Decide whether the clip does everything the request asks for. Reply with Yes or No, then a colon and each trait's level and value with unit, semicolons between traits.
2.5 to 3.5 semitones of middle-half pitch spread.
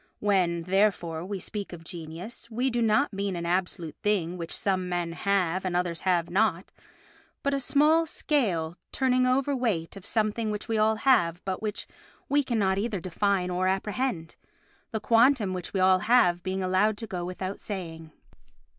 No: average, 4.0 semitones